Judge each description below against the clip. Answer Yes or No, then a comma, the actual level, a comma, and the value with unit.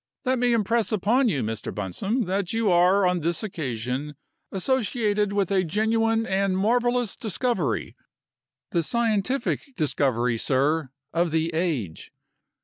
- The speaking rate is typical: No, slow, 130 wpm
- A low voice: No, high, 190 Hz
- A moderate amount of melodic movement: No, wide, 6.4 semitones